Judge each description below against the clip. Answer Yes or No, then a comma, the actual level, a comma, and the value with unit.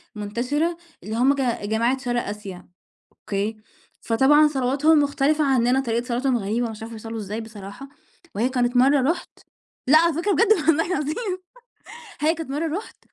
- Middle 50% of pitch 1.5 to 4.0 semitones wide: No, average, 5.0 semitones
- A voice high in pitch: Yes, very high, 260 Hz